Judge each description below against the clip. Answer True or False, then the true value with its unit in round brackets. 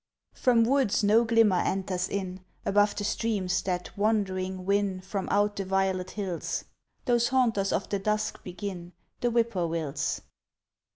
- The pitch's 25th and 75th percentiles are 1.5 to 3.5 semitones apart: True (2.7 semitones)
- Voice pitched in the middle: False (200 Hz)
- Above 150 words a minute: False (135 wpm)